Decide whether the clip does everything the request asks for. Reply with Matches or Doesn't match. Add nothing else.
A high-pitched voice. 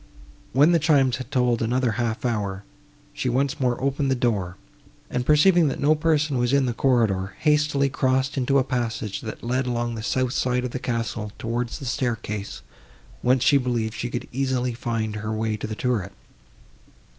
Doesn't match